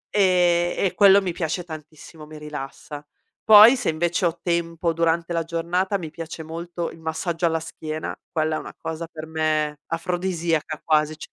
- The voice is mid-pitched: Yes, medium, 165 Hz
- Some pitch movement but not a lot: No, narrow, 1.7 semitones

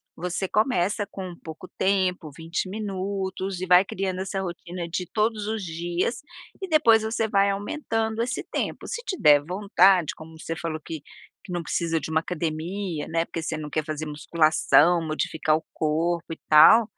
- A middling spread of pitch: Yes, average, 3.7 semitones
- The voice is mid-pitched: Yes, medium, 180 Hz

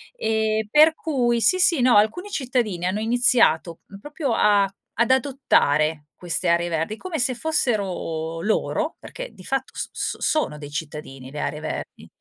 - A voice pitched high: Yes, high, 220 Hz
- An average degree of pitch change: No, wide, 8.2 semitones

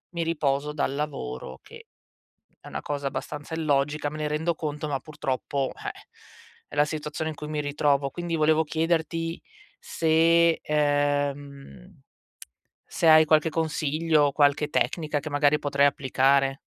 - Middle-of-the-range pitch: Yes, medium, 150 Hz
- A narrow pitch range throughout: Yes, narrow, 1.8 semitones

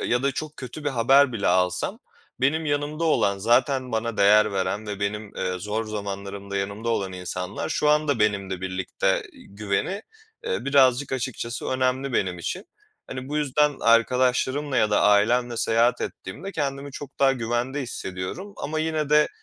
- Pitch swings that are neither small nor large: No, wide, 5.7 semitones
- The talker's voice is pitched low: Yes, low, 120 Hz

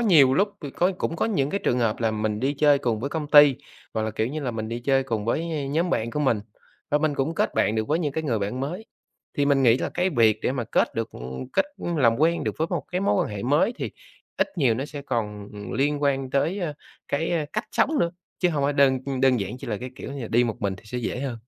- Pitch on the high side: No, low, 135 Hz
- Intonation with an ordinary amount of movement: Yes, average, 4.7 semitones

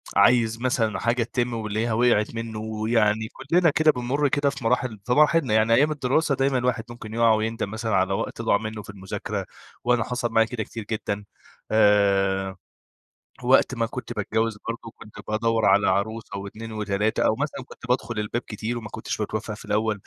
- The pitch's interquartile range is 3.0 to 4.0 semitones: No, narrow, 2.5 semitones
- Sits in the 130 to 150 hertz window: No, low, 115 Hz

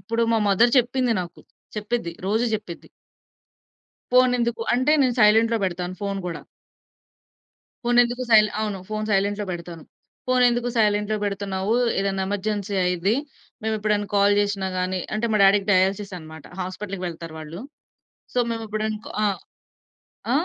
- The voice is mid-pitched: No, high, 205 Hz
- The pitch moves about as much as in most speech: Yes, average, 3.0 semitones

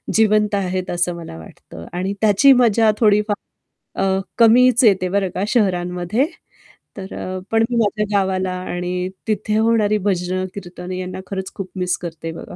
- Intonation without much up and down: No, average, 3.0 semitones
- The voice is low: No, high, 190 Hz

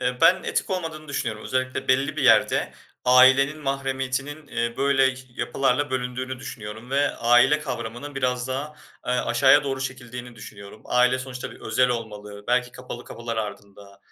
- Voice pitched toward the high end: No, low, 130 Hz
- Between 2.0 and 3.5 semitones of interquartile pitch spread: Yes, narrow, 2.4 semitones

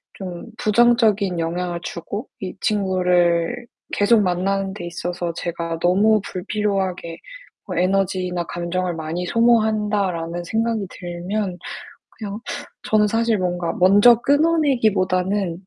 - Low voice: No, high, 190 Hz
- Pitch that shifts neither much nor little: Yes, average, 3.4 semitones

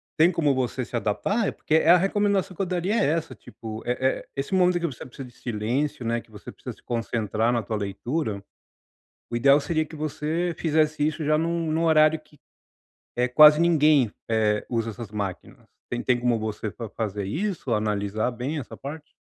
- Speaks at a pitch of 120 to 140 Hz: Yes, low, 135 Hz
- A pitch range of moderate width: No, wide, 6.1 semitones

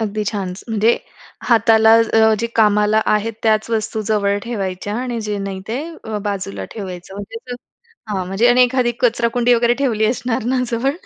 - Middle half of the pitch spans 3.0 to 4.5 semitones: No, narrow, 2.5 semitones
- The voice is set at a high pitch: Yes, high, 220 Hz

